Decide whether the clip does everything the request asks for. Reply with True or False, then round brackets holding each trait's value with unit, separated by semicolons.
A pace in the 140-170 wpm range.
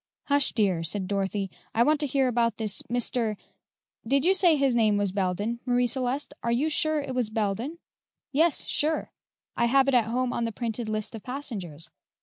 False (195 wpm)